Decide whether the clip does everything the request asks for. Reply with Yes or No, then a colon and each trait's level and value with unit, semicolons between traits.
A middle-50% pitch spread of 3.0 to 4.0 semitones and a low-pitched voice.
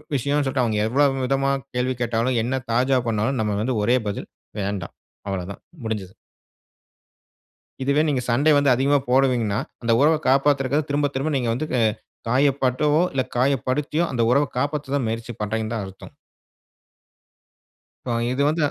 Yes: average, 3.6 semitones; low, 130 Hz